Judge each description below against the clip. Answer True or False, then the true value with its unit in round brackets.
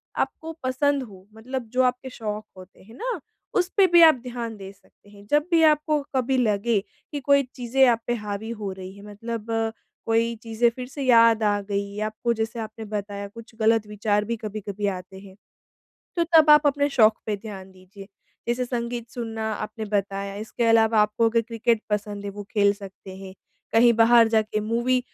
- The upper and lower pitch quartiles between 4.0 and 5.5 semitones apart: False (3.1 semitones)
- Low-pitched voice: False (225 Hz)